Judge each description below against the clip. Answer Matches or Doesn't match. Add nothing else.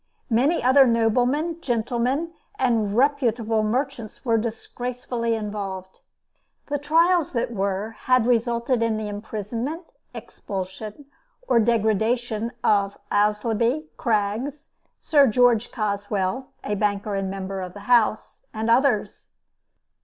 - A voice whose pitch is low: Doesn't match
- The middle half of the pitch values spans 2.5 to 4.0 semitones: Matches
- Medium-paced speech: Doesn't match